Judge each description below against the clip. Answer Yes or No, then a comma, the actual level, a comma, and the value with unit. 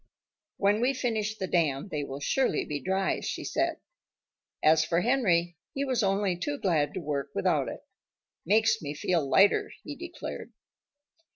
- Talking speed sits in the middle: Yes, average, 160 wpm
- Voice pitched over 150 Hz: Yes, high, 190 Hz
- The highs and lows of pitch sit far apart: Yes, wide, 6.1 semitones